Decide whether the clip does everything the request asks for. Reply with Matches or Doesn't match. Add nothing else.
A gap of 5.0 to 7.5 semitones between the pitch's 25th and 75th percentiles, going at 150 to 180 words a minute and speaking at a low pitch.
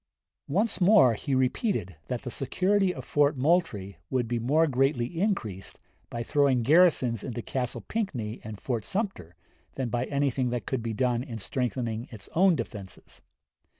Matches